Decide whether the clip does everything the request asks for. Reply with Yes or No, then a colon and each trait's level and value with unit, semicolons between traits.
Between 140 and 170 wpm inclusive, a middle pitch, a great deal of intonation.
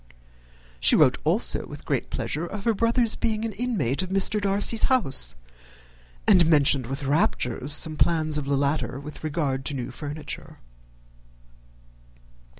Yes: average, 145 wpm; medium, 155 Hz; wide, 6.2 semitones